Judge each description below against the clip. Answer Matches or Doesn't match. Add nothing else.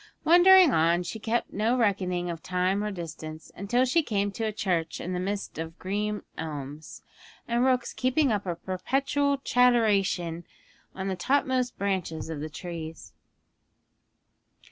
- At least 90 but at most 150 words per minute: Matches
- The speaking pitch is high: Matches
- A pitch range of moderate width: Doesn't match